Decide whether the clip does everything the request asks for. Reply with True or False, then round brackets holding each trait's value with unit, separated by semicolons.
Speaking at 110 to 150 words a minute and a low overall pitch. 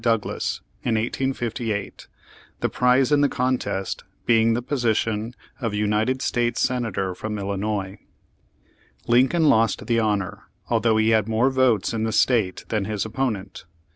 True (140 wpm; 115 Hz)